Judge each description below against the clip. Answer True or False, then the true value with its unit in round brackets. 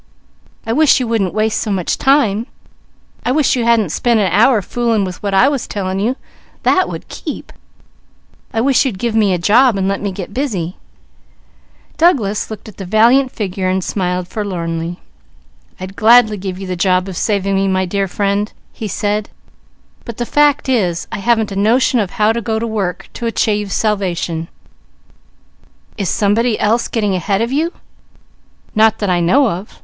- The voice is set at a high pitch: True (210 Hz)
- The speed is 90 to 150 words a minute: False (170 wpm)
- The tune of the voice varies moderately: True (3.6 semitones)